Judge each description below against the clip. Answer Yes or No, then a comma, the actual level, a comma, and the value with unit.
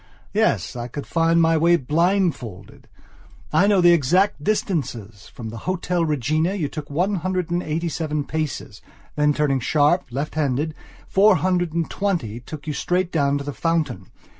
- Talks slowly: No, average, 165 wpm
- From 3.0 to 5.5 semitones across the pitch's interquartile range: Yes, average, 3.8 semitones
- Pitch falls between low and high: Yes, medium, 160 Hz